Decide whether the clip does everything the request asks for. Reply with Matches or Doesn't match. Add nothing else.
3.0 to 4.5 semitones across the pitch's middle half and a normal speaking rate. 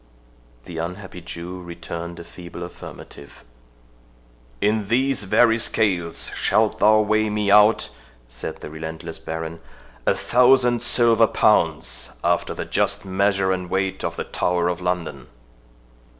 Doesn't match